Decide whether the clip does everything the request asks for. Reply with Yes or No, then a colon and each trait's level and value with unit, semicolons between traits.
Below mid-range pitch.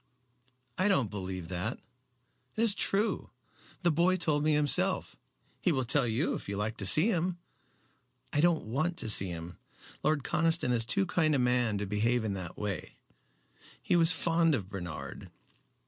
Yes: low, 130 Hz